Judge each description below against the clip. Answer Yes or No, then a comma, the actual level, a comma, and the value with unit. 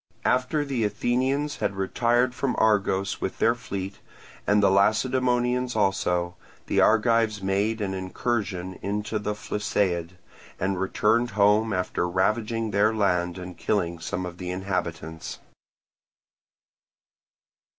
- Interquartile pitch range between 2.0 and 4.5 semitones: Yes, average, 3.6 semitones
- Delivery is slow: Yes, slow, 120 wpm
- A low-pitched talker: Yes, low, 105 Hz